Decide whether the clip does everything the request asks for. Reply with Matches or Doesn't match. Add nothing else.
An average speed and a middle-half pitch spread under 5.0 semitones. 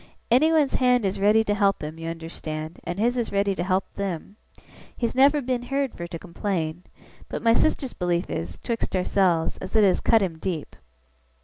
Doesn't match